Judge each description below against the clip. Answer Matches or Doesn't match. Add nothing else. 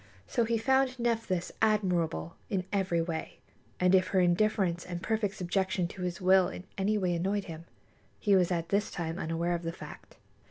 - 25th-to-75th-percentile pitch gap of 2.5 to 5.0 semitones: Matches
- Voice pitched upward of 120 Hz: Matches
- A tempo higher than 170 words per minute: Matches